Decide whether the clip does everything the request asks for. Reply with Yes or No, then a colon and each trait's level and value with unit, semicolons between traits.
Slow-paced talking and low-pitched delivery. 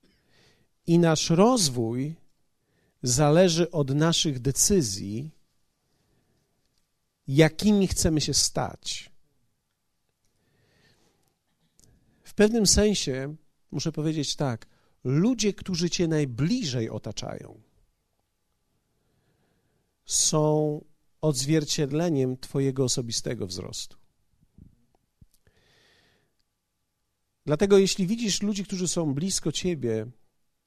No: slow, 70 wpm; medium, 145 Hz